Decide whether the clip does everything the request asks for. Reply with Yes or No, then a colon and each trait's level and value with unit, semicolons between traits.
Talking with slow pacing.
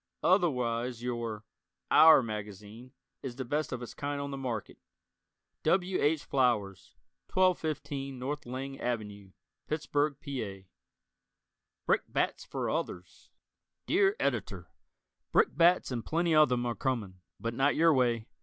Yes: slow, 125 wpm